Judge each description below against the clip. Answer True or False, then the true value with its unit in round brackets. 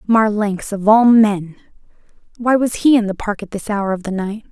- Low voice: False (210 Hz)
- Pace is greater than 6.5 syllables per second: False (4.8 syllables/s)